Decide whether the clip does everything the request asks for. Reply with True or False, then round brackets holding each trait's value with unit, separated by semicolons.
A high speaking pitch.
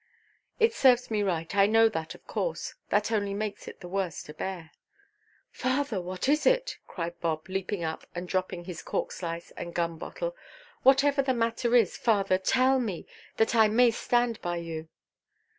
True (200 Hz)